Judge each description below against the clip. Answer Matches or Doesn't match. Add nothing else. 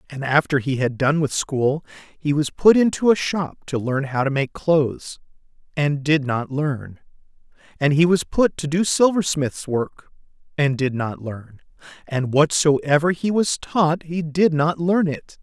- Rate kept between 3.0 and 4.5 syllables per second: Matches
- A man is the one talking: Matches